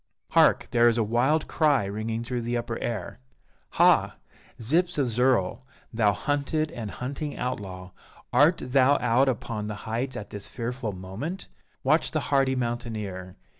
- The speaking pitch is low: Yes, low, 120 Hz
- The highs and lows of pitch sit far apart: No, average, 4.0 semitones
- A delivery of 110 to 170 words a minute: Yes, average, 150 wpm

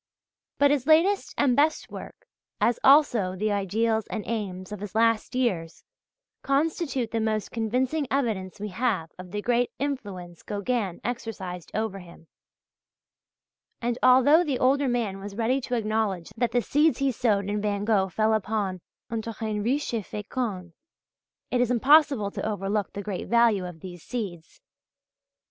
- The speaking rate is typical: Yes, average, 155 wpm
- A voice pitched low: No, high, 220 Hz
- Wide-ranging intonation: No, average, 4.1 semitones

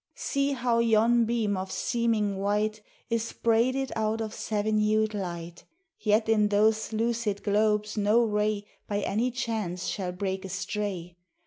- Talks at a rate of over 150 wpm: No, average, 140 wpm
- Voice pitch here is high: Yes, high, 215 Hz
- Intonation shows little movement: Yes, narrow, 2.0 semitones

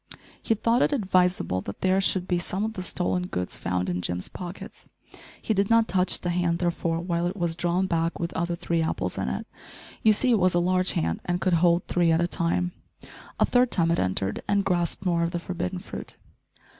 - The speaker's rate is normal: No, fast, 220 wpm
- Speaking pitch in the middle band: Yes, medium, 175 Hz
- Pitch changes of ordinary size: No, narrow, 1.9 semitones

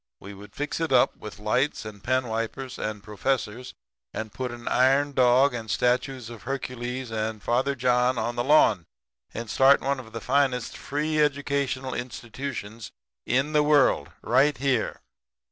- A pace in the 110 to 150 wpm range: No, average, 160 wpm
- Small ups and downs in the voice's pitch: No, average, 3.2 semitones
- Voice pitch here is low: Yes, low, 125 Hz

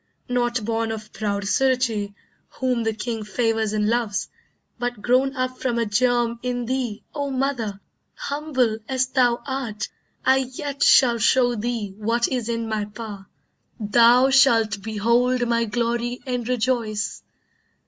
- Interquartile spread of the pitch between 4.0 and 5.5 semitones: No, narrow, 2.6 semitones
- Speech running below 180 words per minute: Yes, average, 140 wpm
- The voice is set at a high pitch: Yes, high, 235 Hz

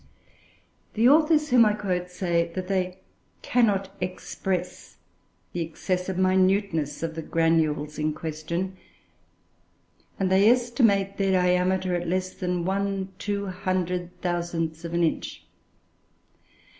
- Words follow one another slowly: Yes, slow, 105 wpm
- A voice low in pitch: No, medium, 185 Hz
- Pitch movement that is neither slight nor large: No, narrow, 2.3 semitones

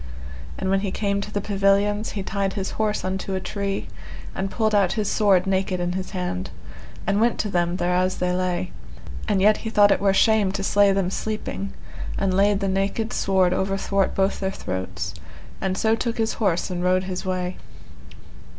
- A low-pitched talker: No, high, 195 Hz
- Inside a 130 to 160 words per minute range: No, average, 190 wpm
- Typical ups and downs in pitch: No, narrow, 1.7 semitones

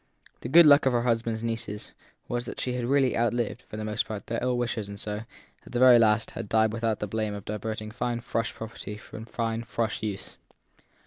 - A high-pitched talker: No, low, 115 Hz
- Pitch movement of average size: No, narrow, 2.0 semitones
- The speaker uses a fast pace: Yes, fast, 220 wpm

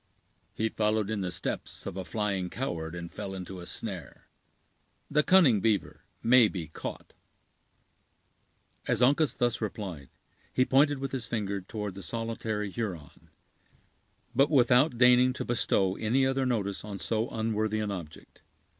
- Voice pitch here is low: Yes, low, 110 Hz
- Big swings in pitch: No, average, 4.2 semitones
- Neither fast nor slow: Yes, average, 145 wpm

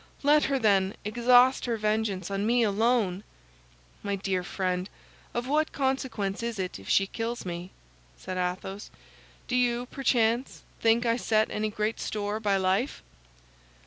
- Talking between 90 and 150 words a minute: Yes, average, 145 wpm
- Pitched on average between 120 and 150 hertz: No, high, 215 Hz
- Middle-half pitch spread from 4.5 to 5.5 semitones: No, average, 3.7 semitones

